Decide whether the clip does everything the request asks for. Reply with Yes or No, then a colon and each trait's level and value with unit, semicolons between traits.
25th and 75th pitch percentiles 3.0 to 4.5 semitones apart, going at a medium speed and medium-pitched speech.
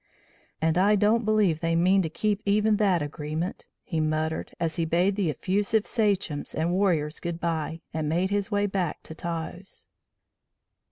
Yes: average, 4.0 semitones; average, 160 wpm; medium, 175 Hz